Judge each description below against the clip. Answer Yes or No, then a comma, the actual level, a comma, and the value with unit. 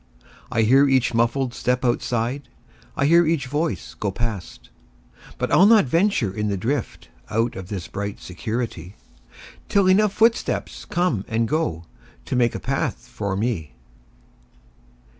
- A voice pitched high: No, low, 120 Hz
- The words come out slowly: Yes, slow, 120 wpm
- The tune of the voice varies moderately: No, wide, 6.2 semitones